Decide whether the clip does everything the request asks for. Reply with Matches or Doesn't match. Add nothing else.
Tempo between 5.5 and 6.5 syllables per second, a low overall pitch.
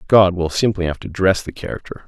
Matches